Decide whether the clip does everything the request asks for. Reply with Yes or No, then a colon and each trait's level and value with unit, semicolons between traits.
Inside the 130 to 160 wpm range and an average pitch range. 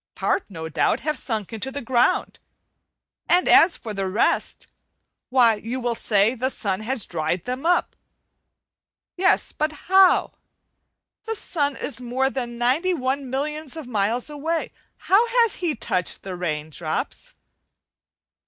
No: average, 145 wpm; wide, 6.2 semitones